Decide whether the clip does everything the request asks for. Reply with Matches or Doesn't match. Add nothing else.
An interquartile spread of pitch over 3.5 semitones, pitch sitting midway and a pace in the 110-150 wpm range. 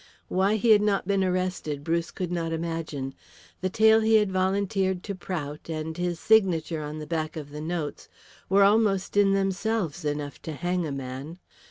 Doesn't match